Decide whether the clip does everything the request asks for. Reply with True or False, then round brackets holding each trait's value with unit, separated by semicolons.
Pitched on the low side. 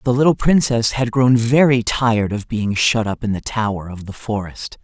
True (115 Hz)